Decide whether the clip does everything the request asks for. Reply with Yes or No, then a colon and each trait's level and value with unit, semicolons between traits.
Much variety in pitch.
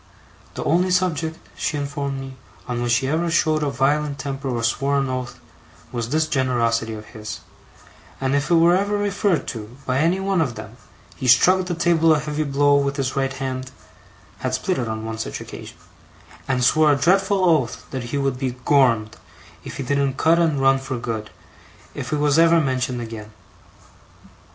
No: average, 4.0 semitones